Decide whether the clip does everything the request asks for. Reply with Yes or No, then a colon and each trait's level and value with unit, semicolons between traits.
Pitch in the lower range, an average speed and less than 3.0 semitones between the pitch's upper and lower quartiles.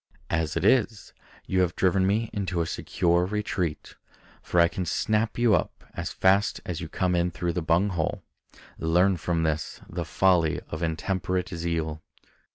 Yes: very low, 90 Hz; average, 165 wpm; narrow, 2.6 semitones